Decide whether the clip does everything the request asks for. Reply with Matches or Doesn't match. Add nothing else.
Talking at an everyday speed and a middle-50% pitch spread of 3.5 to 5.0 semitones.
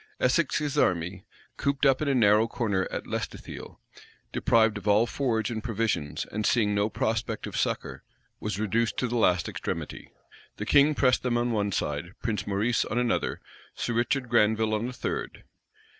Doesn't match